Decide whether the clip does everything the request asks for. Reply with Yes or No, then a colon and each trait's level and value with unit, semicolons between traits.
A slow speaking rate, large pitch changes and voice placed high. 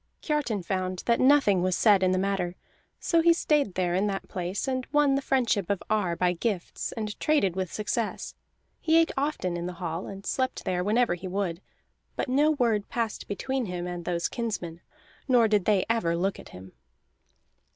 No: average, 190 wpm; wide, 5.8 semitones; high, 200 Hz